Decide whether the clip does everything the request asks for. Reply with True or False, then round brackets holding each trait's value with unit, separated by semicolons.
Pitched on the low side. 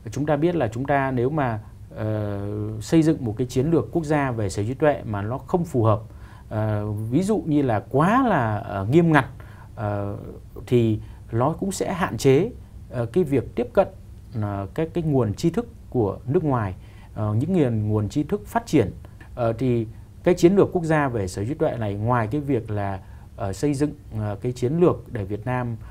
True (115 Hz)